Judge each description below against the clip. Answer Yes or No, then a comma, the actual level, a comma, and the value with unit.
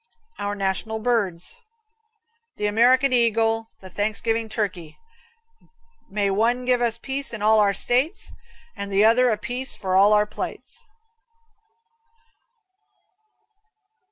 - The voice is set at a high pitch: Yes, high, 220 Hz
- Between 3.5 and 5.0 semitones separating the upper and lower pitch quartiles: No, average, 3.1 semitones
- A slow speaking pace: Yes, slow, 115 wpm